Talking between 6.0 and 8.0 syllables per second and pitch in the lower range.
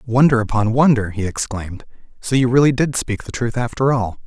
No: 5.6 syllables/s; low, 120 Hz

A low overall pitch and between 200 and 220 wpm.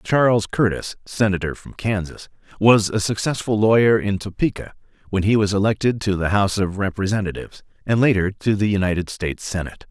No: low, 100 Hz; average, 165 wpm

